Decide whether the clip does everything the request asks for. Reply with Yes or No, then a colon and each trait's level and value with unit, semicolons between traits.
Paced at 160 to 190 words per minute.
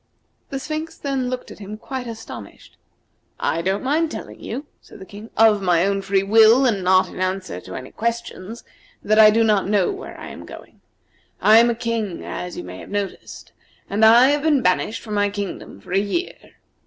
No: fast, 205 wpm